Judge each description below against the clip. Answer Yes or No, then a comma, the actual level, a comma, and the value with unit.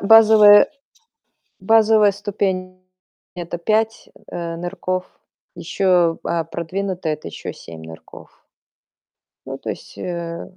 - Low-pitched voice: No, medium, 185 Hz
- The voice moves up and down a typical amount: Yes, average, 3.3 semitones